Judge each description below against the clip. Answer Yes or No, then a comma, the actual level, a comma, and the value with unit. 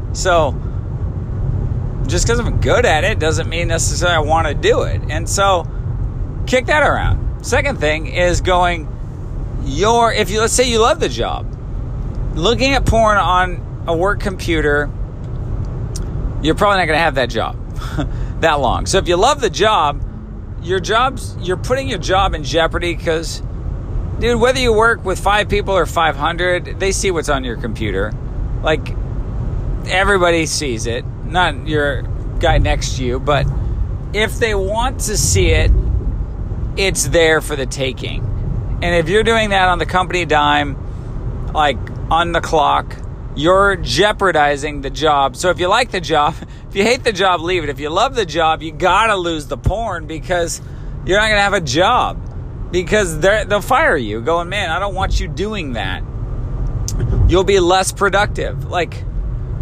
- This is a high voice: No, medium, 140 Hz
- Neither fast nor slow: Yes, average, 170 wpm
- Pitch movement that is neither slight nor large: No, wide, 7.5 semitones